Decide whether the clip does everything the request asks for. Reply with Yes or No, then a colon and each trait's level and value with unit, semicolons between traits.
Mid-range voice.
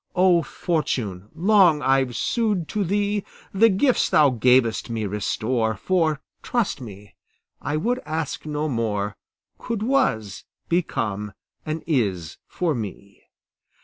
Yes: medium, 150 Hz